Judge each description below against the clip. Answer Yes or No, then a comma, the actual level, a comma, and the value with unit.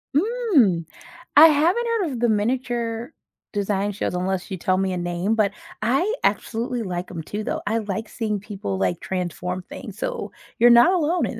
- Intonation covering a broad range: Yes, wide, 5.8 semitones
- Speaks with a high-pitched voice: Yes, high, 215 Hz